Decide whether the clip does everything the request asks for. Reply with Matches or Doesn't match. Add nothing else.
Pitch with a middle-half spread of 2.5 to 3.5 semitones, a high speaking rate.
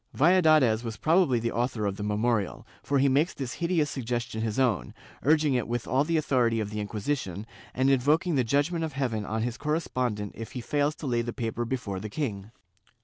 Doesn't match